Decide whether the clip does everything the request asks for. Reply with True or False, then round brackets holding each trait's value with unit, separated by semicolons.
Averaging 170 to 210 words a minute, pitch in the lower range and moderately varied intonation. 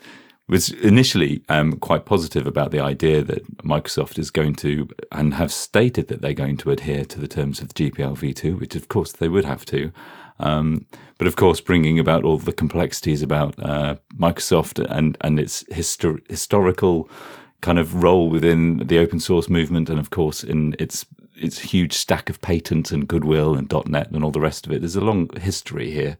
False (195 wpm; 80 Hz; 2.0 semitones)